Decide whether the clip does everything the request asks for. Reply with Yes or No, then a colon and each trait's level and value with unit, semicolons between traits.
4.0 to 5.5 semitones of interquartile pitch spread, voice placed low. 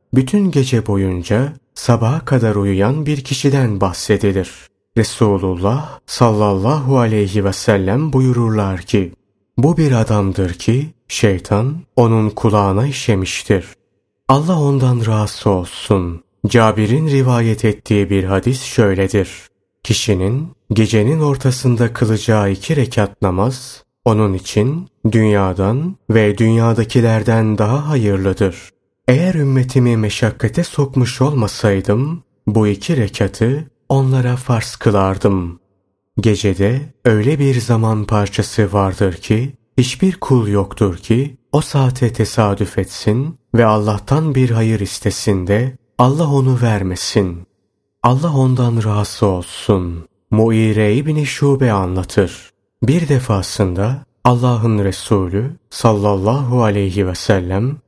Yes: average, 4.5 semitones; low, 110 Hz